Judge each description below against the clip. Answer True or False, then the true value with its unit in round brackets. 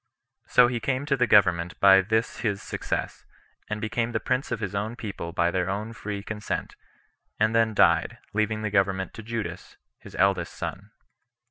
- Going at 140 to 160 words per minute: False (175 wpm)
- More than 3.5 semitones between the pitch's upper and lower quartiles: False (2.7 semitones)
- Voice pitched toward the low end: True (105 Hz)